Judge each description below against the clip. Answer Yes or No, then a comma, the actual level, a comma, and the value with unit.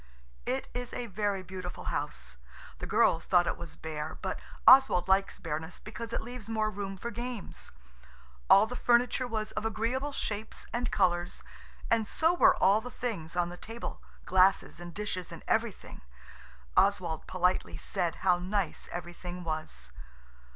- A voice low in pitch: No, high, 195 Hz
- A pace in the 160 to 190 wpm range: No, average, 150 wpm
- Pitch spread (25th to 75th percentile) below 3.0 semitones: No, average, 4.4 semitones